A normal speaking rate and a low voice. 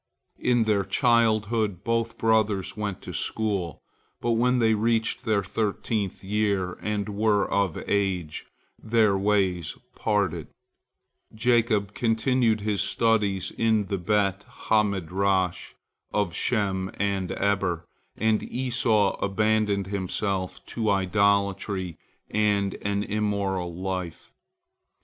No: slow, 110 wpm; low, 100 Hz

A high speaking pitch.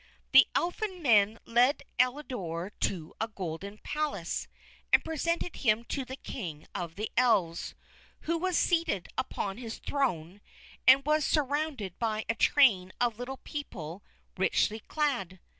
Yes: high, 235 Hz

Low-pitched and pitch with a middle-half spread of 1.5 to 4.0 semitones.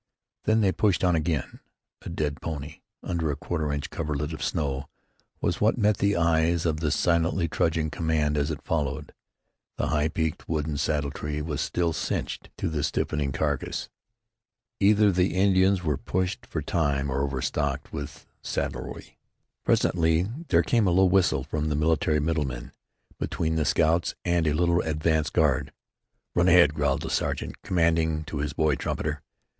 Yes: very low, 80 Hz; narrow, 2.6 semitones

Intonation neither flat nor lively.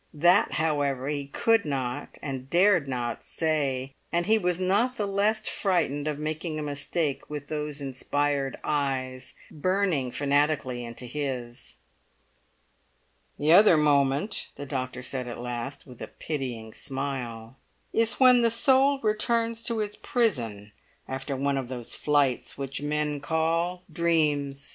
Yes: average, 4.8 semitones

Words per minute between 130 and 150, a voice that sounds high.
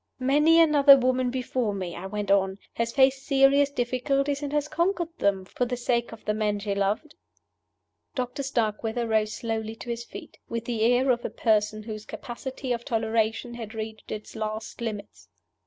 No: average, 175 wpm; high, 235 Hz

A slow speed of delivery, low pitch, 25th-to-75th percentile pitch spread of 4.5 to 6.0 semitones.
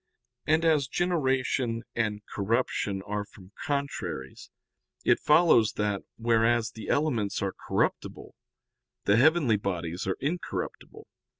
Yes: slow, 110 wpm; low, 115 Hz; wide, 5.6 semitones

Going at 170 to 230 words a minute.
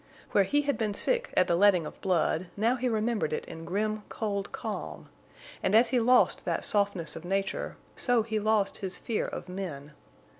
Yes: average, 190 wpm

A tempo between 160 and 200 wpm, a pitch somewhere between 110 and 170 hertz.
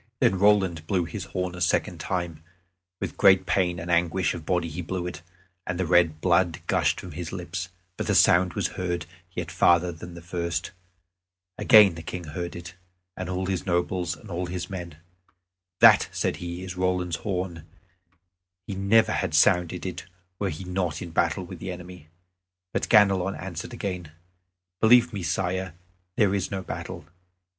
No: average, 170 wpm; very low, 90 Hz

